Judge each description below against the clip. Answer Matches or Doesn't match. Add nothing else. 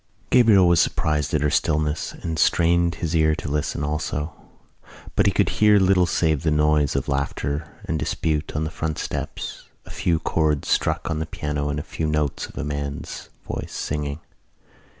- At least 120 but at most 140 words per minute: Doesn't match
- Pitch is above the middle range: Doesn't match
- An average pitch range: Doesn't match